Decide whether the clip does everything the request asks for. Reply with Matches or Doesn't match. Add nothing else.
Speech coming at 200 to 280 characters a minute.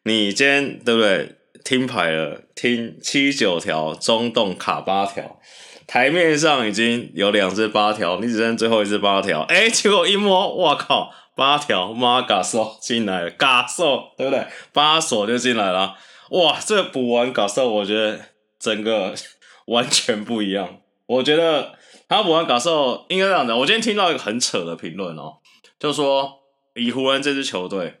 Matches